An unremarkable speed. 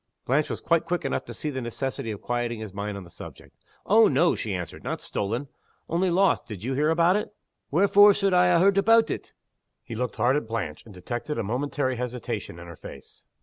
No: fast, 220 wpm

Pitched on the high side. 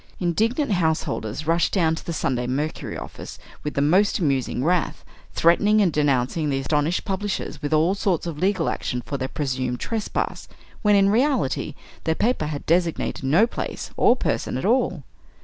No: medium, 165 Hz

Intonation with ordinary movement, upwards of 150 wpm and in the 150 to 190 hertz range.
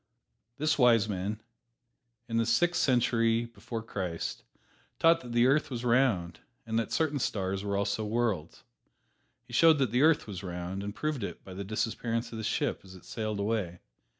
No: average, 3.7 semitones; average, 180 wpm; low, 115 Hz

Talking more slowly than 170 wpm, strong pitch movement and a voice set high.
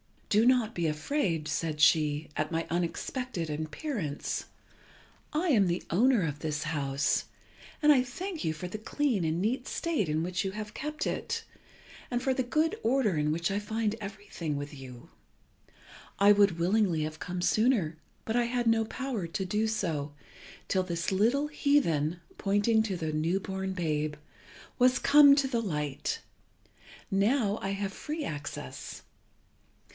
Yes: average, 160 wpm; wide, 7.3 semitones; high, 195 Hz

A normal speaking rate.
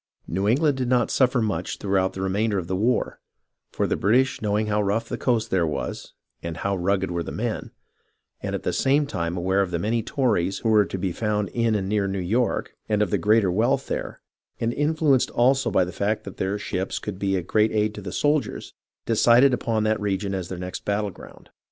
No: fast, 225 wpm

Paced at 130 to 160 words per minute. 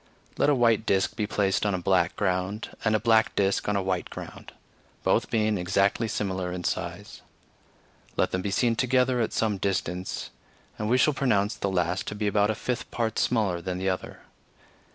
No: average, 195 wpm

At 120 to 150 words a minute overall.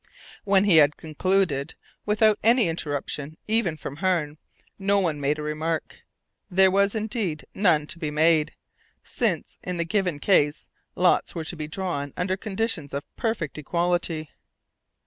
Yes: average, 145 wpm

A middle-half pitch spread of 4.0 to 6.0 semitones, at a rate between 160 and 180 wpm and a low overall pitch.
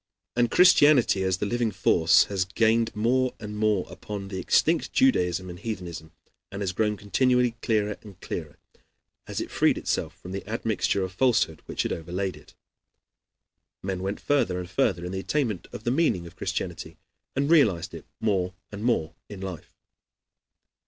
Yes: average, 4.3 semitones; average, 165 wpm; low, 100 Hz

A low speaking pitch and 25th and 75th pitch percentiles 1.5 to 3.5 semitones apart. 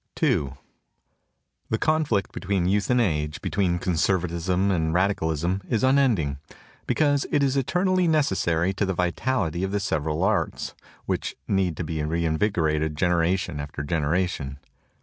No: very low, 90 Hz; average, 4.4 semitones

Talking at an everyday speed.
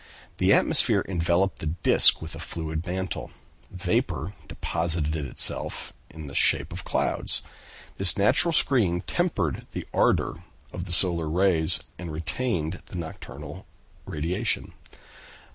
No: slow, 125 wpm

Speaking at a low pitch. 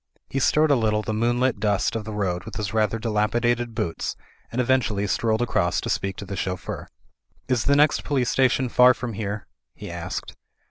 Yes: low, 110 Hz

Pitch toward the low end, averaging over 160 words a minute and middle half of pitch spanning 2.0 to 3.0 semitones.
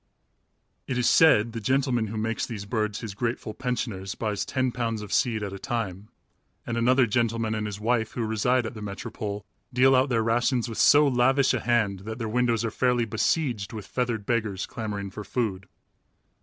Yes: low, 115 Hz; average, 190 wpm; average, 2.7 semitones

